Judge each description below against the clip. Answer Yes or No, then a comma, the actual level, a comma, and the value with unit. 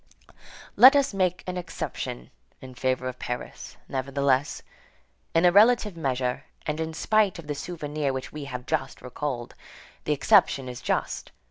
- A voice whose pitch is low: No, medium, 145 Hz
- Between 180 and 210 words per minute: No, average, 150 wpm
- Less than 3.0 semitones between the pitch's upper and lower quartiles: No, average, 5.3 semitones